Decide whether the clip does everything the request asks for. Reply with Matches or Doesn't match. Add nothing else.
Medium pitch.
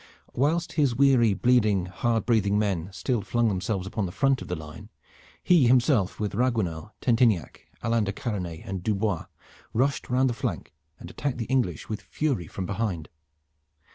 Doesn't match